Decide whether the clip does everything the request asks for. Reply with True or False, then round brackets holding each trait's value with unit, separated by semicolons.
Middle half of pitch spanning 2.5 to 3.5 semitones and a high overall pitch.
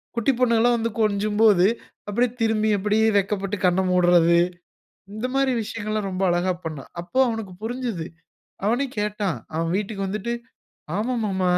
True (3.2 semitones; 210 Hz)